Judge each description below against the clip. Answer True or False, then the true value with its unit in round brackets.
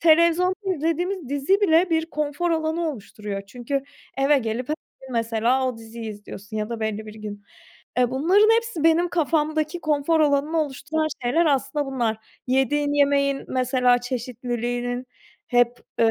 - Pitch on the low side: False (275 Hz)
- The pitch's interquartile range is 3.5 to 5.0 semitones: True (4.7 semitones)